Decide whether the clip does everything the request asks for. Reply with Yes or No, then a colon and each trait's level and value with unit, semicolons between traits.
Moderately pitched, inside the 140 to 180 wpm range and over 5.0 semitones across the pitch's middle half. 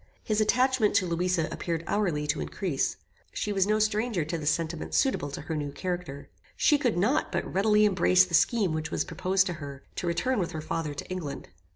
No: medium, 180 Hz; fast, 205 wpm; wide, 5.4 semitones